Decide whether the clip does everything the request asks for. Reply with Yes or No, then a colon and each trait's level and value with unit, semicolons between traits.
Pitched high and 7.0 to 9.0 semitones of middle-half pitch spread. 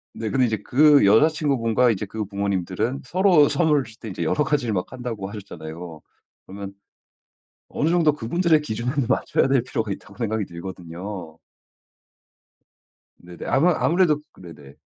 No: low, 115 Hz; wide, 7.4 semitones